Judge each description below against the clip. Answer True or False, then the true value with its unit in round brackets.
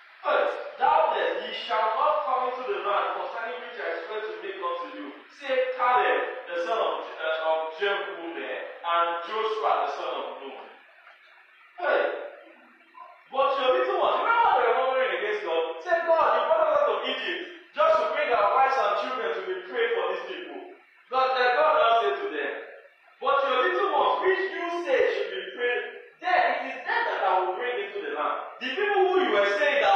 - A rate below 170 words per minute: False (205 wpm)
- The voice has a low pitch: False (300 Hz)